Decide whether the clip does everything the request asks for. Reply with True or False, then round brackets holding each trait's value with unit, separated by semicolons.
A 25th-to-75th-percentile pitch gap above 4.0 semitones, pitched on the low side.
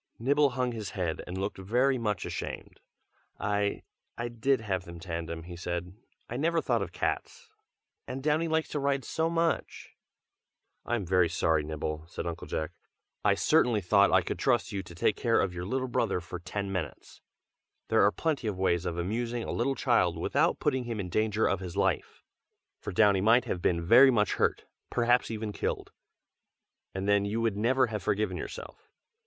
True (5.3 semitones; 105 Hz)